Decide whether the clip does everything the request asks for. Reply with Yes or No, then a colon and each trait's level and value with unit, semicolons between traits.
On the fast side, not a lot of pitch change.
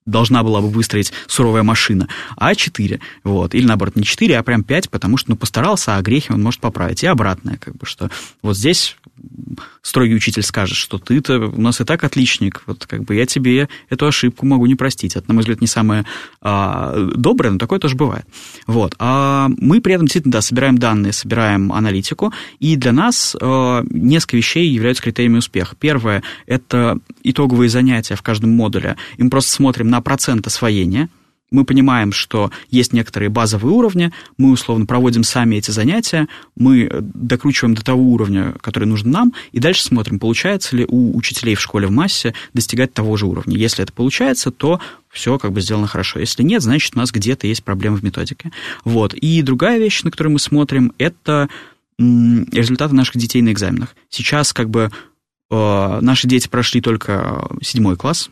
No: fast, 180 wpm; average, 3.5 semitones